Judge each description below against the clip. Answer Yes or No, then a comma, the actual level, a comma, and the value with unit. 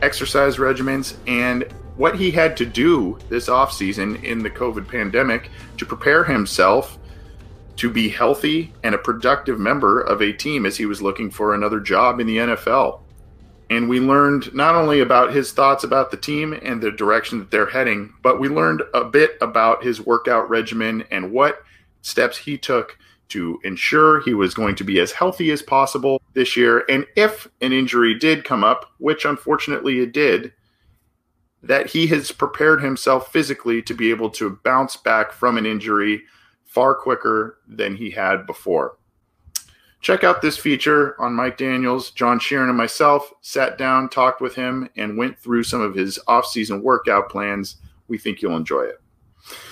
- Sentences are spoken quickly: No, average, 175 wpm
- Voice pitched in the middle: No, low, 125 Hz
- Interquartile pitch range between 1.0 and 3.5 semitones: No, average, 4.1 semitones